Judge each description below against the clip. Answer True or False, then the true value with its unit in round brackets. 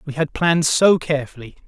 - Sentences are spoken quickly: False (180 wpm)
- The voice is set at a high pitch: False (150 Hz)